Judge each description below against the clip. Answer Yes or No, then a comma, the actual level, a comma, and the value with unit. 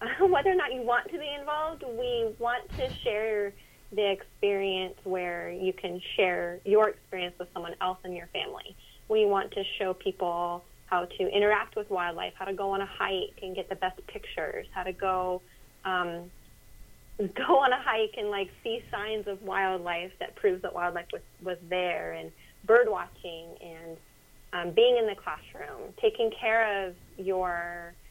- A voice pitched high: Yes, high, 195 Hz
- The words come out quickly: No, average, 175 wpm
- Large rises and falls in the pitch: No, average, 4.0 semitones